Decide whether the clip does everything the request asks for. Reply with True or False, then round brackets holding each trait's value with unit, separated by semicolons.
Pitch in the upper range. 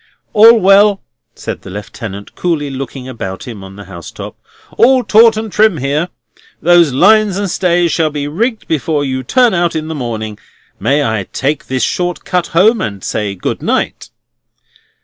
False (155 Hz)